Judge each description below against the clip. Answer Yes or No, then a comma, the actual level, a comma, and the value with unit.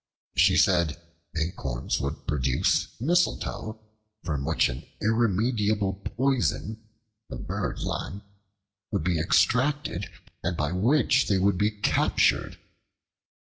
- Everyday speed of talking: No, slow, 105 wpm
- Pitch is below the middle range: Yes, low, 100 Hz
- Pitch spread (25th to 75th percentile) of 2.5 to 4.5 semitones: No, wide, 5.5 semitones